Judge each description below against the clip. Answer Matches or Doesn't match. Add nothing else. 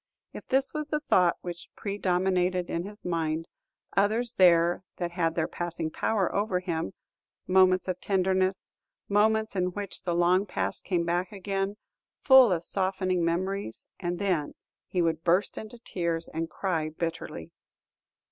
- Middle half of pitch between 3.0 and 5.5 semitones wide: Doesn't match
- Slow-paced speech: Doesn't match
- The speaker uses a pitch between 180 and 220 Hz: Matches